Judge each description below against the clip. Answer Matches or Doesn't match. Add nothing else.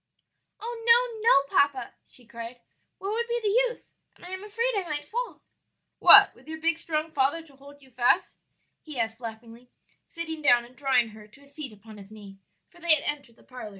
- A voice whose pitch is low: Doesn't match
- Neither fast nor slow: Doesn't match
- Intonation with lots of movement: Matches